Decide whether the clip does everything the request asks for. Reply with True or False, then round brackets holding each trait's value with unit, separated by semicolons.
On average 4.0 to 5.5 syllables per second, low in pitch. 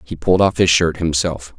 True (5.4 syllables/s; 80 Hz)